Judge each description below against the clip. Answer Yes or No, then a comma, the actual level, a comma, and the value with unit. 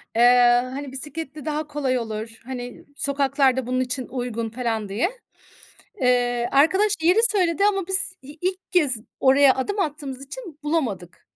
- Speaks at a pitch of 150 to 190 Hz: No, very high, 270 Hz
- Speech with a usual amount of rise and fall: Yes, average, 4.6 semitones